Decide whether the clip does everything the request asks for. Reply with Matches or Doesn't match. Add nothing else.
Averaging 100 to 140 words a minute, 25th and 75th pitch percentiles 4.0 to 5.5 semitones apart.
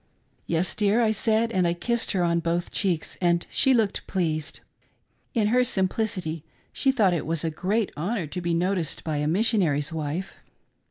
Doesn't match